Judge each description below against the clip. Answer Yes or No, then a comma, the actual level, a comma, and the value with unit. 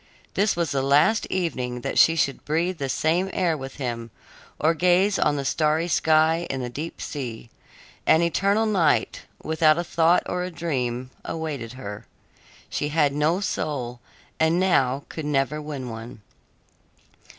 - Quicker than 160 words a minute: No, average, 155 wpm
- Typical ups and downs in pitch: Yes, average, 4.2 semitones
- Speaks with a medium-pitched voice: Yes, medium, 155 Hz